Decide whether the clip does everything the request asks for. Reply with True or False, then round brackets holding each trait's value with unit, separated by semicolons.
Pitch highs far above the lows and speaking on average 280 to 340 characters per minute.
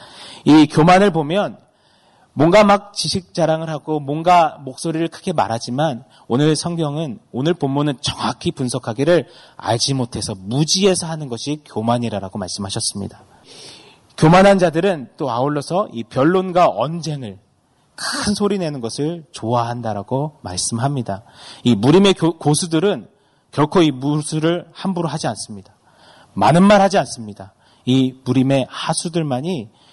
True (6.1 semitones; 300 characters per minute)